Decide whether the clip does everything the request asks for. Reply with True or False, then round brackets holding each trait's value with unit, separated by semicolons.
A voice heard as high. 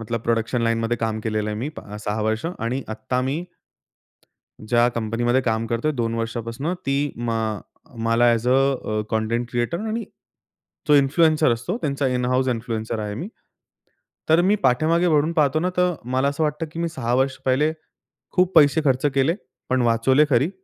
False (125 Hz)